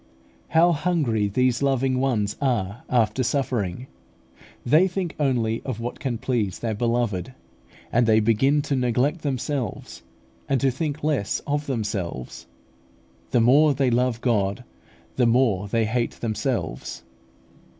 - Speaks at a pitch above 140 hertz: No, low, 125 Hz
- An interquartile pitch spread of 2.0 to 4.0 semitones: Yes, average, 3.7 semitones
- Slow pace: Yes, slow, 130 wpm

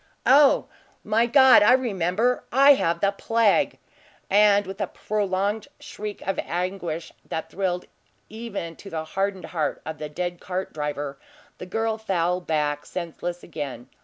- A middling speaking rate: Yes, average, 145 wpm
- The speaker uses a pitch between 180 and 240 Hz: Yes, high, 190 Hz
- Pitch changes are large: No, average, 4.3 semitones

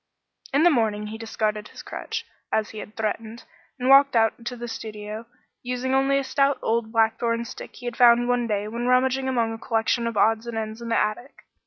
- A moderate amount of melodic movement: No, narrow, 2.3 semitones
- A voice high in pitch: Yes, high, 230 Hz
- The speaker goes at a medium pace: No, fast, 210 wpm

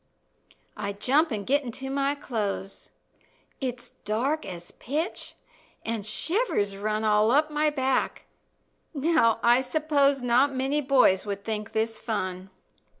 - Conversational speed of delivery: No, slow, 130 wpm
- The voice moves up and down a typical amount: Yes, average, 4.9 semitones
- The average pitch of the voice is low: No, high, 245 Hz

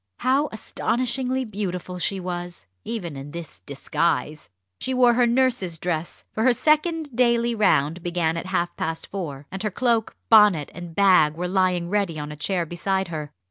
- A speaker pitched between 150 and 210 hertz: Yes, medium, 185 Hz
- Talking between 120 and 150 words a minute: No, average, 170 wpm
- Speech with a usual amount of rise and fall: No, wide, 5.8 semitones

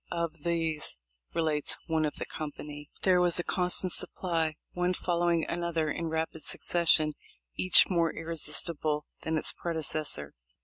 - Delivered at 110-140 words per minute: Yes, slow, 135 wpm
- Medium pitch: Yes, medium, 165 Hz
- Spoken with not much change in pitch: Yes, narrow, 1.8 semitones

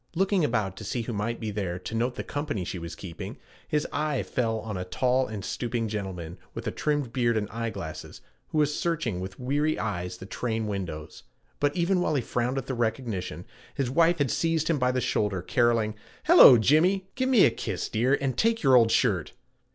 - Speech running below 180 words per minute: No, fast, 205 wpm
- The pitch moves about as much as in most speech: No, wide, 5.9 semitones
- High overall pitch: No, low, 120 Hz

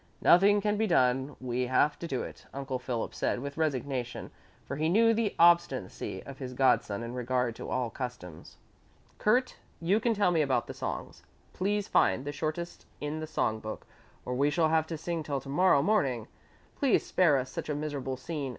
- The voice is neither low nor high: Yes, medium, 145 Hz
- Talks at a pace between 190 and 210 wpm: Yes, average, 195 wpm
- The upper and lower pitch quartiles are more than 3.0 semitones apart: Yes, average, 5.1 semitones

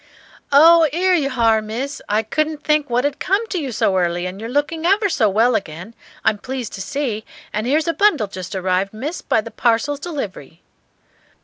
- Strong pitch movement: Yes, wide, 6.4 semitones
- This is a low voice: No, very high, 250 Hz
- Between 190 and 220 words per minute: Yes, average, 195 wpm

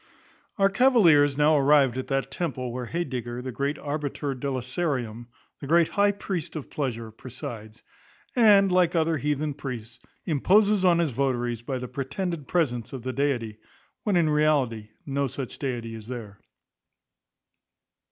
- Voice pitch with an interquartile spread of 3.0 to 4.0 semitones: No, average, 5.0 semitones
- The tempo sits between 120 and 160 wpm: Yes, average, 145 wpm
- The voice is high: No, medium, 140 Hz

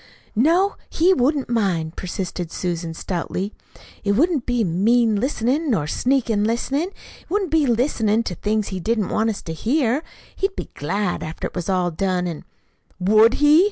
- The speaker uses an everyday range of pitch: No, wide, 6.6 semitones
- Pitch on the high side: Yes, high, 220 Hz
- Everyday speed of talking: Yes, average, 175 wpm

